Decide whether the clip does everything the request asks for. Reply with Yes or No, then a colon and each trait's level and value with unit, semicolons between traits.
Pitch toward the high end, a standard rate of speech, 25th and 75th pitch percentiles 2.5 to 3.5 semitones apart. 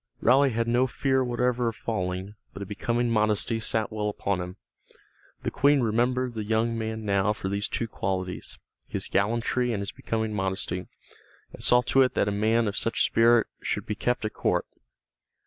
No: low, 110 Hz; average, 180 wpm; average, 2.8 semitones